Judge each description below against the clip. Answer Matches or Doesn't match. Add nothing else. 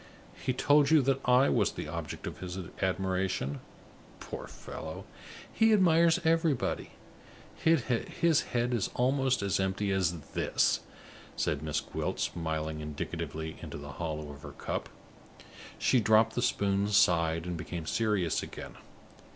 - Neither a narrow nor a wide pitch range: Doesn't match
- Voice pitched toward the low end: Matches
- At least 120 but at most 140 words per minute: Matches